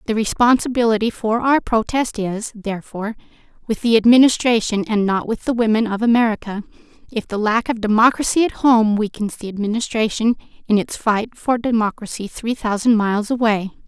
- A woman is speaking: Yes, female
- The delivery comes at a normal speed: Yes, average, 155 wpm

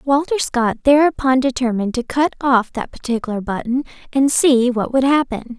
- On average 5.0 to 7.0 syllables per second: Yes, 5.1 syllables/s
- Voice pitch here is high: Yes, very high, 255 Hz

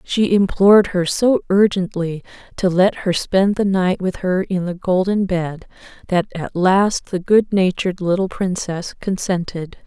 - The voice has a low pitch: No, medium, 185 Hz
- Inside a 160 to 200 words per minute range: No, average, 150 wpm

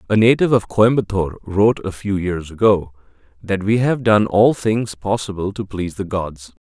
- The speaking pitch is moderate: No, low, 100 Hz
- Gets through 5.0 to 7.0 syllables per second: Yes, 5.2 syllables/s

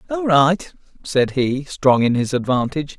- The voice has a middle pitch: Yes, medium, 145 Hz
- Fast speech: No, average, 160 wpm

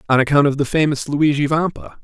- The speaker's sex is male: Yes, male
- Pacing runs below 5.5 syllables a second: No, 6.0 syllables/s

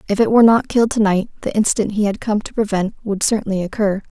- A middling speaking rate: No, fast, 230 wpm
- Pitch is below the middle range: No, high, 210 Hz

